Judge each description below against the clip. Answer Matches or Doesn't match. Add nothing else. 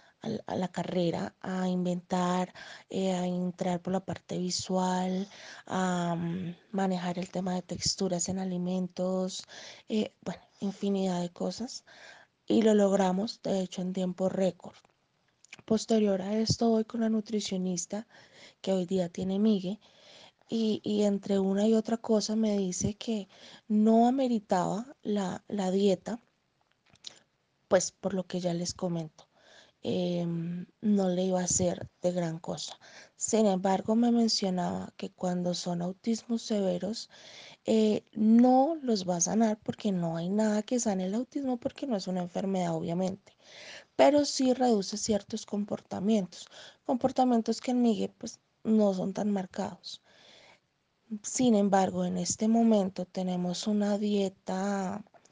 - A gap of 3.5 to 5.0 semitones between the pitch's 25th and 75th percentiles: Doesn't match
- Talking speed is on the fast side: Doesn't match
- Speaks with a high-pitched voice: Matches